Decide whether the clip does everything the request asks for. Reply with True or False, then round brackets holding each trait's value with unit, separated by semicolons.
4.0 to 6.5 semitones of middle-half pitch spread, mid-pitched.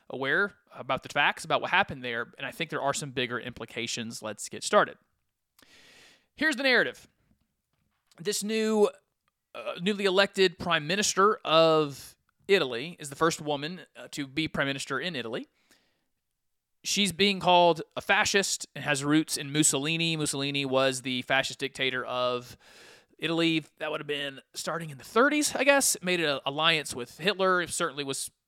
True (5.2 semitones; 155 Hz)